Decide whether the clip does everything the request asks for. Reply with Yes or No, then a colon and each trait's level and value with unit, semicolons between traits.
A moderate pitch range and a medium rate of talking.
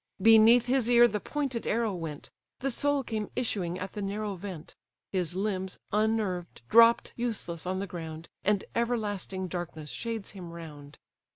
Yes: average, 4.6 semitones; average, 155 wpm